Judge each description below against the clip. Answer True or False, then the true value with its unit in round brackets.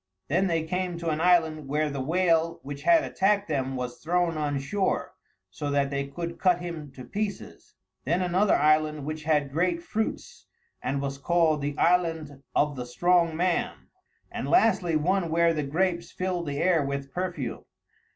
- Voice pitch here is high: False (165 Hz)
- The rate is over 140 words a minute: True (170 wpm)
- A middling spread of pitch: True (3.8 semitones)